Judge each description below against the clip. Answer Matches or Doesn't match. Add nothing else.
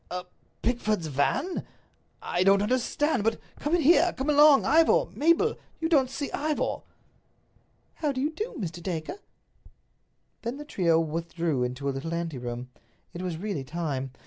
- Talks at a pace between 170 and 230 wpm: Doesn't match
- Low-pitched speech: Doesn't match